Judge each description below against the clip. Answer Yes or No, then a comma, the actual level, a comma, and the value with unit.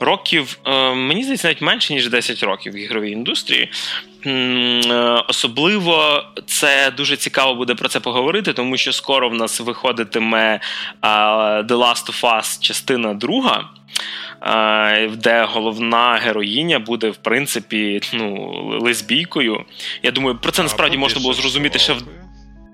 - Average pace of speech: Yes, average, 130 wpm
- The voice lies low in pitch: Yes, low, 120 Hz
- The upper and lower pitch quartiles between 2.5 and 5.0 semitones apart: Yes, average, 3.4 semitones